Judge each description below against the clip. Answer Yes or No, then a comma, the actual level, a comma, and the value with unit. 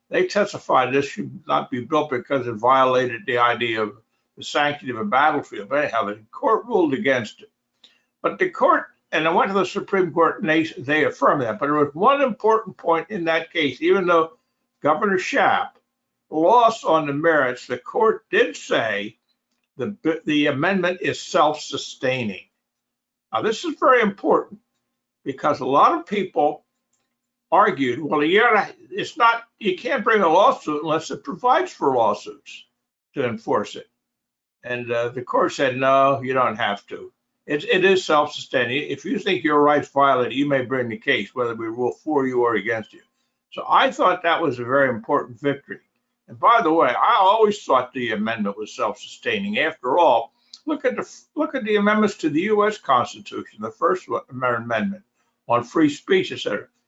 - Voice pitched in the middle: Yes, medium, 160 Hz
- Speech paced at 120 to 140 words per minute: No, average, 175 wpm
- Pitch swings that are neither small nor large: No, wide, 9.0 semitones